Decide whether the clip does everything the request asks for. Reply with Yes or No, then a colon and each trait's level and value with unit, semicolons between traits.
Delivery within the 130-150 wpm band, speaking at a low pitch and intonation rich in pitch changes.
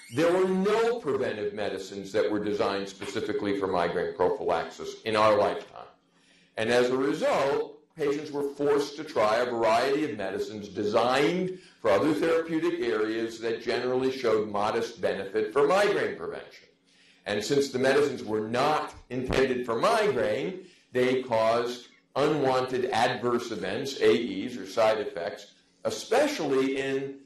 Yes: slow, 135 wpm; low, 130 Hz; wide, 8.9 semitones